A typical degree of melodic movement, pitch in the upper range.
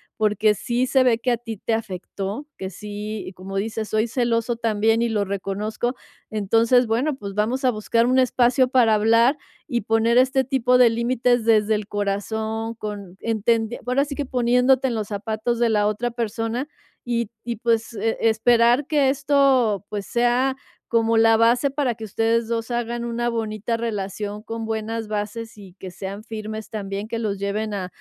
No: narrow, 2.3 semitones; high, 225 Hz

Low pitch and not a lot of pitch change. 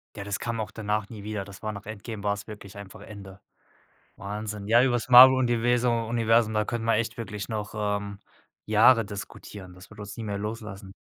Yes: low, 105 Hz; narrow, 2.1 semitones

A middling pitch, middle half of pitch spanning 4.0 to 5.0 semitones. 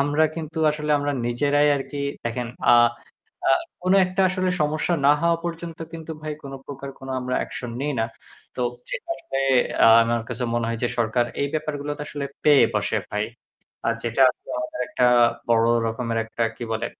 Yes: medium, 145 Hz; average, 4.5 semitones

